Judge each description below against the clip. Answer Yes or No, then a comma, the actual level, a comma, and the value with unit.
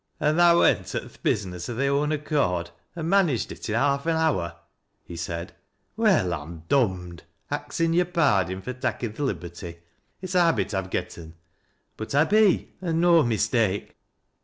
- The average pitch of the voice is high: No, low, 125 Hz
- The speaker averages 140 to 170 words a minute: No, average, 185 wpm